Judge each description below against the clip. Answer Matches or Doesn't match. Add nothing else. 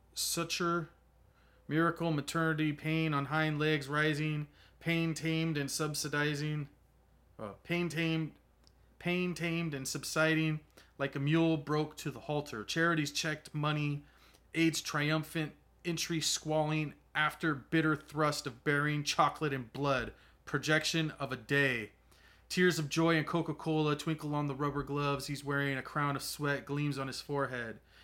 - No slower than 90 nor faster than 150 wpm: Matches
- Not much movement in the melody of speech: Matches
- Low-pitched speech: Doesn't match